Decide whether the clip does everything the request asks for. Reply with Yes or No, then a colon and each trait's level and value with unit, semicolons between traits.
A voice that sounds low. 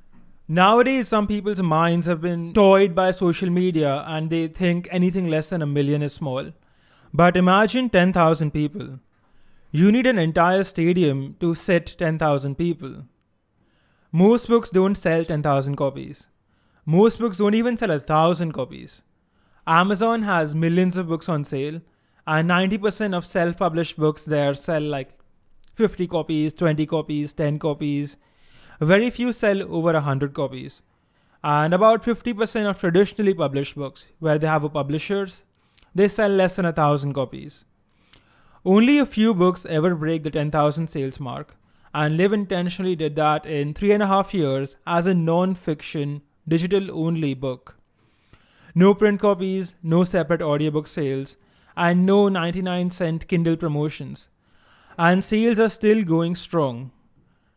No: medium, 170 Hz